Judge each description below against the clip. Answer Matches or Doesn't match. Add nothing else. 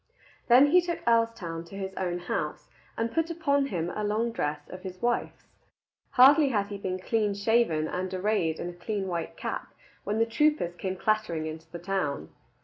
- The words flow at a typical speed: Matches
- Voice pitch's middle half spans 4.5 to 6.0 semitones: Matches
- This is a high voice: Matches